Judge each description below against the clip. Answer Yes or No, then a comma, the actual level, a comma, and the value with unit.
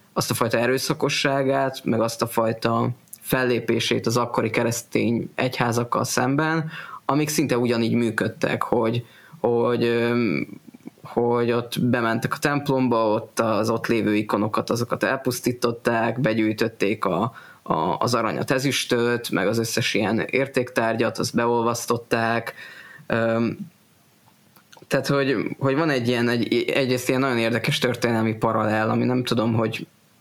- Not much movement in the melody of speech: Yes, narrow, 2.3 semitones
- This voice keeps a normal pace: Yes, average, 125 wpm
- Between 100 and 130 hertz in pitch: Yes, low, 120 Hz